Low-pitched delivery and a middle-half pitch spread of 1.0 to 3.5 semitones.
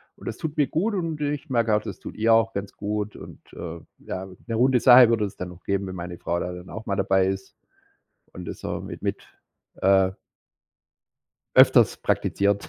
No: low, 105 Hz; average, 4.5 semitones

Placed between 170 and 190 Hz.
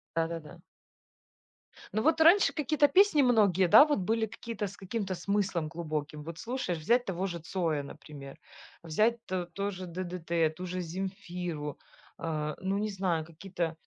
Yes: medium, 185 Hz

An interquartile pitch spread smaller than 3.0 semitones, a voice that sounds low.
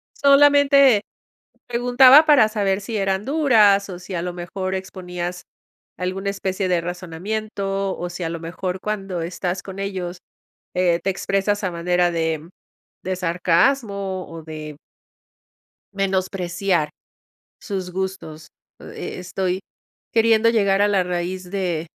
No: narrow, 2.4 semitones; high, 190 Hz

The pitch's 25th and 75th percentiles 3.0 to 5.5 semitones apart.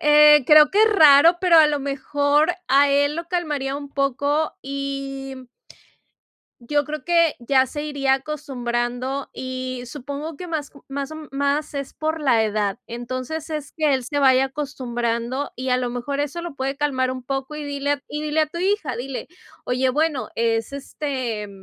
No: narrow, 2.6 semitones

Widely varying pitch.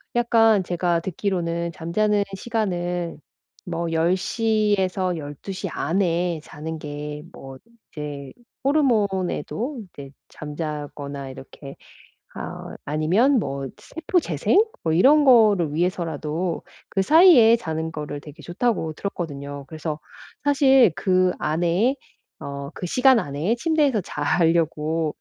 Yes: wide, 5.9 semitones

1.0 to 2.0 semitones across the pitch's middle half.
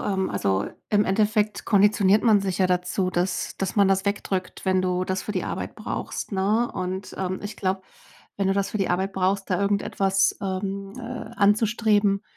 Yes: narrow, 1.5 semitones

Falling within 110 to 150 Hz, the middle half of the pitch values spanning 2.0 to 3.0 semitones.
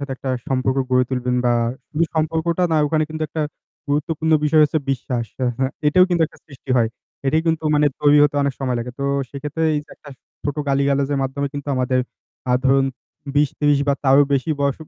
Yes: medium, 140 Hz; narrow, 2.5 semitones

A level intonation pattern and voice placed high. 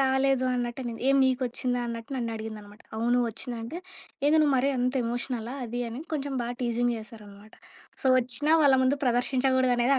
Yes: narrow, 2.3 semitones; high, 245 Hz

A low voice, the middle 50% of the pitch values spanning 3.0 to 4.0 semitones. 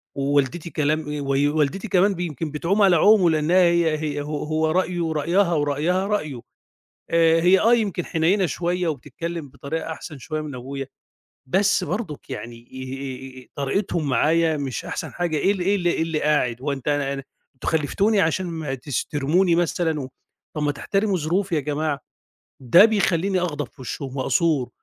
No: medium, 160 Hz; average, 3.7 semitones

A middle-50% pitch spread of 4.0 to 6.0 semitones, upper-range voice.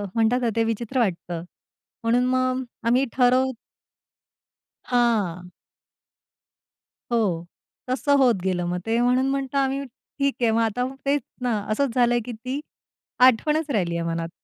No: average, 3.0 semitones; high, 240 Hz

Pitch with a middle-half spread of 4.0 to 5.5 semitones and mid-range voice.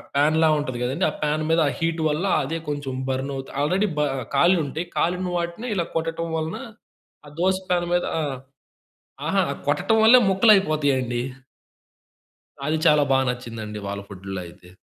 Yes: average, 4.7 semitones; medium, 155 Hz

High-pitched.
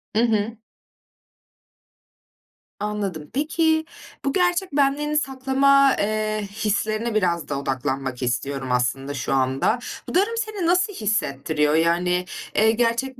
Yes: high, 215 Hz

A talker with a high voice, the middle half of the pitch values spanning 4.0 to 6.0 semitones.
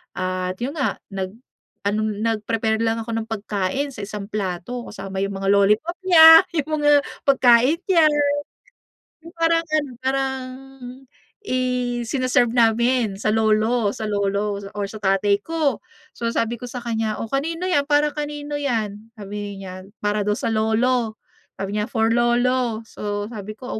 Yes: high, 225 Hz; average, 4.3 semitones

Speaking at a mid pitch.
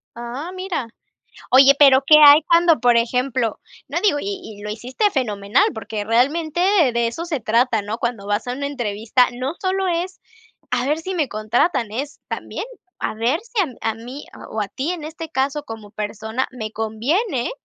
No: very high, 255 Hz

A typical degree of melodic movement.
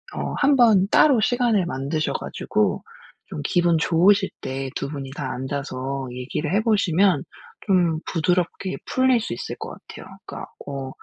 No: wide, 6.8 semitones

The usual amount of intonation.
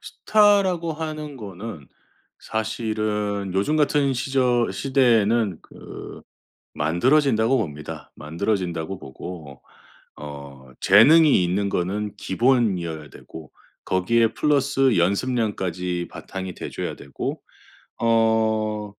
No: wide, 6.2 semitones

